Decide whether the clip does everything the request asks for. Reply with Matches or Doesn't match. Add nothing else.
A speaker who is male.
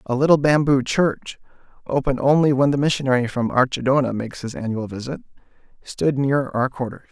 Matches